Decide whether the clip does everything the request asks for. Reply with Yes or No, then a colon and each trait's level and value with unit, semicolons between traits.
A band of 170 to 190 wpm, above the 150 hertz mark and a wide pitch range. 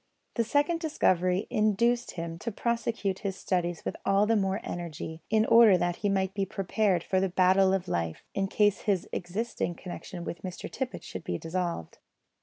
No: average, 180 wpm; high, 190 Hz; average, 3.5 semitones